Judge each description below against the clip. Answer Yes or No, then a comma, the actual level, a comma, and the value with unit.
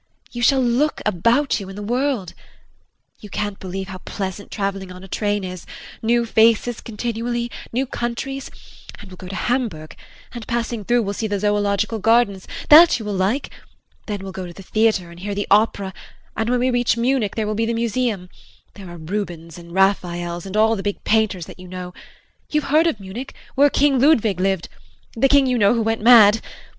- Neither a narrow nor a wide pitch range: Yes, average, 3.8 semitones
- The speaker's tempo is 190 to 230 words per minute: Yes, average, 200 wpm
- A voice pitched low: No, high, 210 Hz